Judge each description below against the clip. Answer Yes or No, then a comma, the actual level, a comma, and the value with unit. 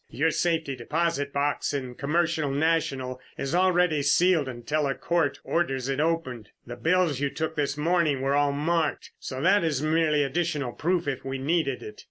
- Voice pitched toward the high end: No, medium, 145 Hz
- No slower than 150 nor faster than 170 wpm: No, average, 180 wpm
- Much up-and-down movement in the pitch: No, average, 3.4 semitones